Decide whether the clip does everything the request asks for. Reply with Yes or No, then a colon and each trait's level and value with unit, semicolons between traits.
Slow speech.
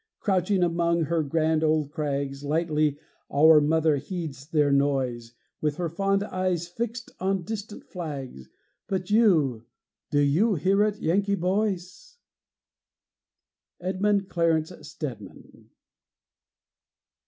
Yes: slow, 110 wpm